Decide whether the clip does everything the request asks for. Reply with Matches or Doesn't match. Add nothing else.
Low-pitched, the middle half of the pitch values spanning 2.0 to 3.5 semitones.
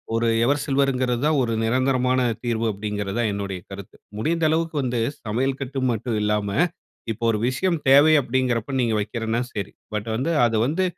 Doesn't match